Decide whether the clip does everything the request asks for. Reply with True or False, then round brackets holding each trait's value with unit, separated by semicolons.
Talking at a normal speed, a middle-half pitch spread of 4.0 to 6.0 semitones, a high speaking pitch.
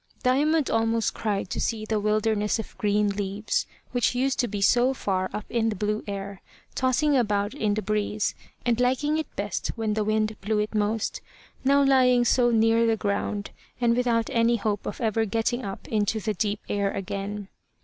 False (185 wpm; 2.8 semitones; 220 Hz)